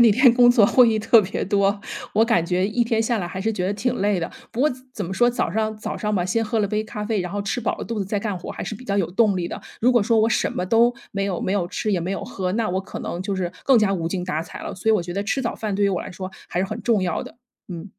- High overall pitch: Yes, high, 205 Hz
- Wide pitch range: No, average, 3.2 semitones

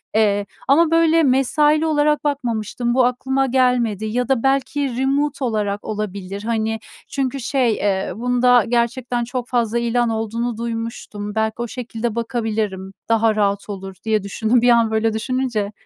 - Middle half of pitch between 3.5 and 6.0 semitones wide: No, average, 2.9 semitones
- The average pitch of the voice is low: No, high, 235 Hz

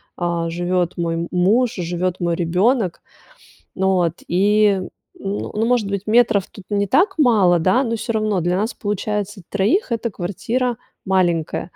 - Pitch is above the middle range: Yes, high, 195 Hz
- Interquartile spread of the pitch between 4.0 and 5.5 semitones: No, average, 3.6 semitones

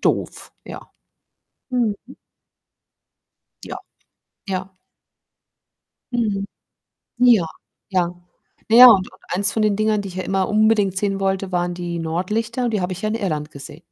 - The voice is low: No, high, 195 Hz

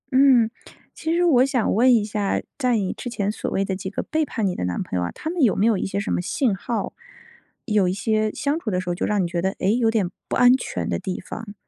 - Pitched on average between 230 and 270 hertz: No, high, 215 Hz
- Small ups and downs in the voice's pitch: No, average, 4.5 semitones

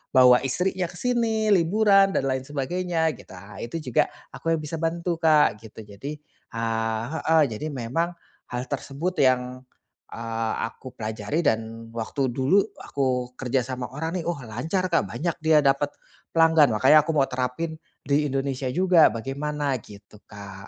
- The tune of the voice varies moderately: No, wide, 5.8 semitones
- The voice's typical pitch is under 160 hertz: Yes, medium, 140 Hz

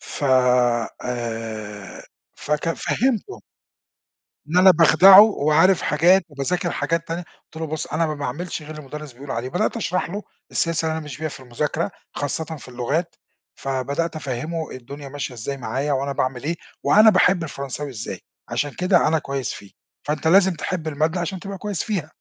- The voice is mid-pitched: Yes, medium, 155 Hz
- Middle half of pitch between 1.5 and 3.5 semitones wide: No, average, 4.2 semitones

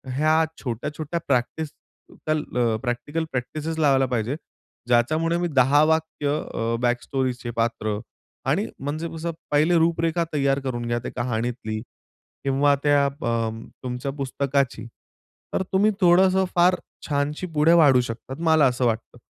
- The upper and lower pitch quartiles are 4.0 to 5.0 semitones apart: Yes, average, 4.6 semitones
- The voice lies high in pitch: No, medium, 140 Hz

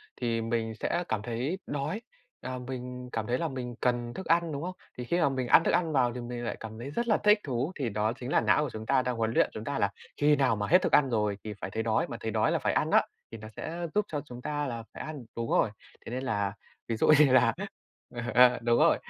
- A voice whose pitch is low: Yes, low, 125 Hz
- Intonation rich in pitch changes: No, average, 4.2 semitones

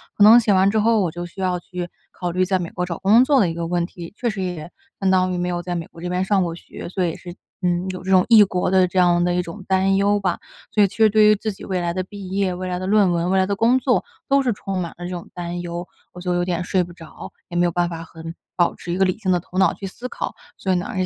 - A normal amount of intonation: No, narrow, 2.1 semitones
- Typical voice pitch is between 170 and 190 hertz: Yes, medium, 185 Hz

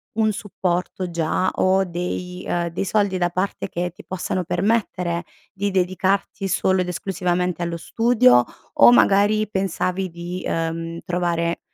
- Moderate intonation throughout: No, narrow, 2.0 semitones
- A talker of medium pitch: Yes, medium, 180 Hz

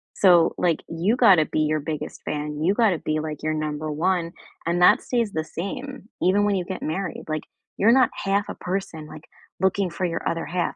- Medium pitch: Yes, medium, 175 Hz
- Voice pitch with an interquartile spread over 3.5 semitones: Yes, average, 4.1 semitones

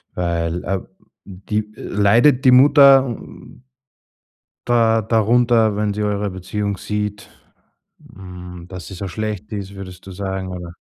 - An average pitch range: Yes, average, 3.2 semitones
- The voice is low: Yes, low, 100 Hz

